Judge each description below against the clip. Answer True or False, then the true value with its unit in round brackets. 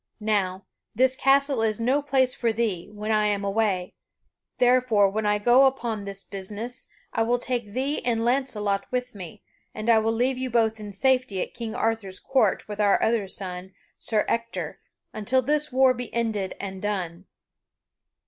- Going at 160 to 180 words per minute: True (170 wpm)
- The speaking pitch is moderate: False (225 Hz)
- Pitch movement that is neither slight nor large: True (3.6 semitones)